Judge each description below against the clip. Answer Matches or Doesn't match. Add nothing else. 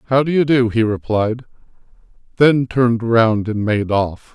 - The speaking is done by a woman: Doesn't match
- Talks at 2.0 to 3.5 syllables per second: Doesn't match